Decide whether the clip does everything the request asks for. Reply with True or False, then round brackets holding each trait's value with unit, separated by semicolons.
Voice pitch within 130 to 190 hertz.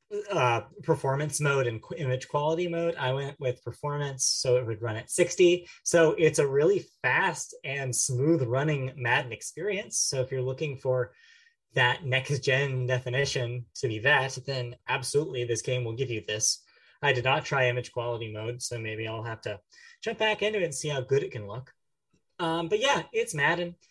True (135 Hz)